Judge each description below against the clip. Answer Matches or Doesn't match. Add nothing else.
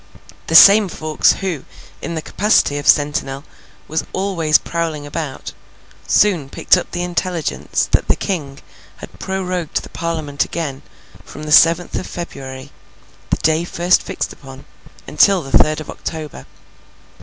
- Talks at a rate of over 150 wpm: Doesn't match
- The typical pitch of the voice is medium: Matches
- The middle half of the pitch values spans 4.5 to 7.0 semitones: Doesn't match